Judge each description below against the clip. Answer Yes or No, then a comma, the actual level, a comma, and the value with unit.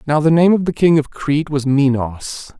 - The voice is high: No, medium, 150 Hz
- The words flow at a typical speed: No, fast, 230 wpm